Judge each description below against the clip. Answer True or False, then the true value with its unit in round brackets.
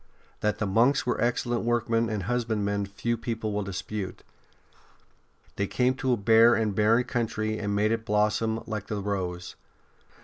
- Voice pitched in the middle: False (110 Hz)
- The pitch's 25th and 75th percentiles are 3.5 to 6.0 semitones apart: False (2.4 semitones)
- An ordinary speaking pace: True (160 wpm)